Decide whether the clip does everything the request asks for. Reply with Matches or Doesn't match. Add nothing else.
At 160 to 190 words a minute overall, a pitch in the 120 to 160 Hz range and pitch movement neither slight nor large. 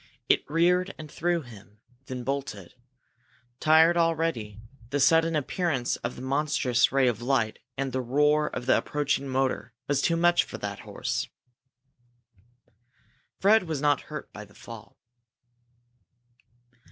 Doesn't match